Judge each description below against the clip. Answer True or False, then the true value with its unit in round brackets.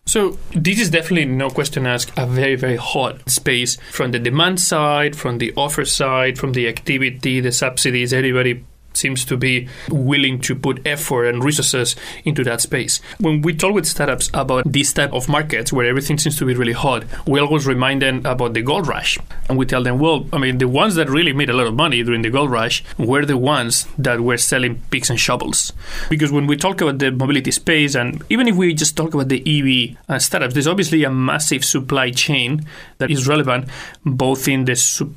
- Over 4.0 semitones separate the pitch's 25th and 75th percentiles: False (2.9 semitones)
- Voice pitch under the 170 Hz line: True (135 Hz)